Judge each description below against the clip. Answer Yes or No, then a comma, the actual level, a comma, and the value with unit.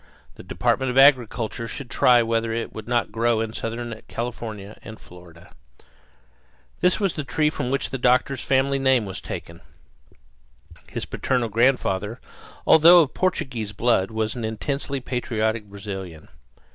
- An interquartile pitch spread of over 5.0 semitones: No, average, 3.4 semitones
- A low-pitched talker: Yes, low, 115 Hz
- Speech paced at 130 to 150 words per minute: Yes, average, 145 wpm